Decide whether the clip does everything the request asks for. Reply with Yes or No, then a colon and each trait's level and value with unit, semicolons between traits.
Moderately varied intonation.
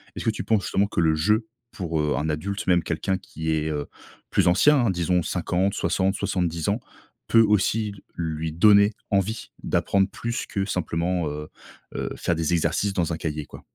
Yes: average, 4.0 semitones